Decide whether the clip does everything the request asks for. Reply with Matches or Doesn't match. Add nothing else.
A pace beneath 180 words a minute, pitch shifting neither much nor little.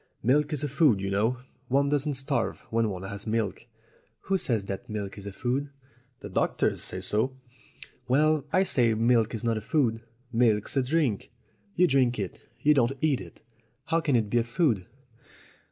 Doesn't match